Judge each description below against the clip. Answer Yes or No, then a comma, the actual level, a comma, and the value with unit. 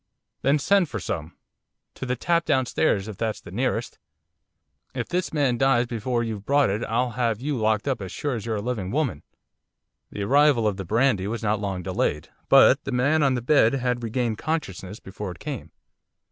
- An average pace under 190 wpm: No, average, 195 wpm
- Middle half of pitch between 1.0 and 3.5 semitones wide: No, average, 4.6 semitones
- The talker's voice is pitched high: No, low, 120 Hz